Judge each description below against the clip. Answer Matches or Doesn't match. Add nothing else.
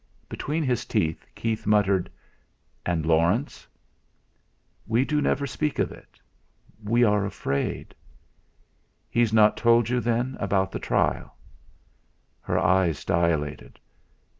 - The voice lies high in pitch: Doesn't match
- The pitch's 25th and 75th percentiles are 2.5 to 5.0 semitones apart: Doesn't match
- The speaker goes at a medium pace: Doesn't match